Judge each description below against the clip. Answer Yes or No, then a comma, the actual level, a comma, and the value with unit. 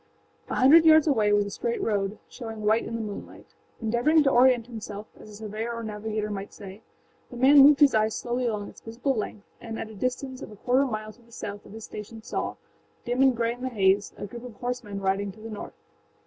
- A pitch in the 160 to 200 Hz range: No, high, 225 Hz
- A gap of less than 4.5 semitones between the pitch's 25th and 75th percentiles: Yes, average, 3.0 semitones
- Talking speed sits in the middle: No, fast, 230 wpm